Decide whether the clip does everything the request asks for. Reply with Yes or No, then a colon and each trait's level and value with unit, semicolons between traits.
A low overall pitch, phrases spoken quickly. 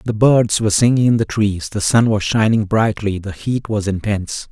Yes: low, 105 Hz; fast, 215 wpm